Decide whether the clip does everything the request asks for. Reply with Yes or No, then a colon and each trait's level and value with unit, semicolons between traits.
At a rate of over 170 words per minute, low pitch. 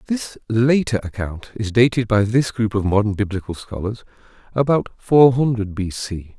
No: average, 160 wpm; low, 110 Hz